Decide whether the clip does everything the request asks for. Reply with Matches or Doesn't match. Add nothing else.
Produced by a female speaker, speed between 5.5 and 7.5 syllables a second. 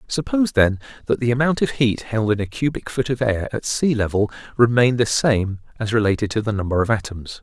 Doesn't match